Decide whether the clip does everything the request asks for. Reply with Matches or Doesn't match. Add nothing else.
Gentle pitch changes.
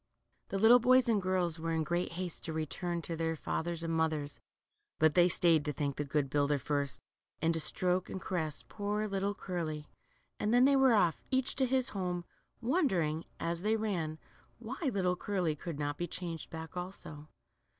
Doesn't match